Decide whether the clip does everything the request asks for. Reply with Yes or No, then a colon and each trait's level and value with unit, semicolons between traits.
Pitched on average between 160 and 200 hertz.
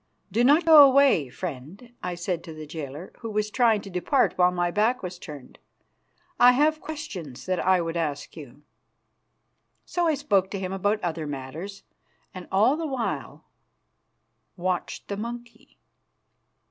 Yes: high, 190 Hz